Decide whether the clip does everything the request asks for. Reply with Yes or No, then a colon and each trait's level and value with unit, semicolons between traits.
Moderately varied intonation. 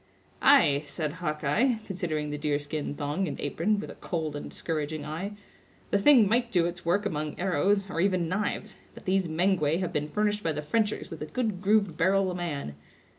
Yes: average, 4.7 semitones